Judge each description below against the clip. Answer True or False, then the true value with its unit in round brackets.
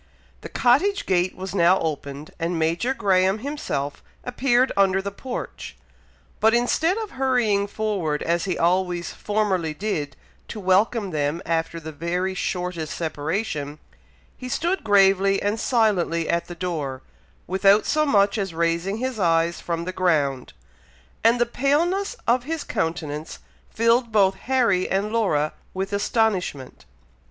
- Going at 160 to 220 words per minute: False (140 wpm)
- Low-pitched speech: False (190 Hz)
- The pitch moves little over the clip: False (5.3 semitones)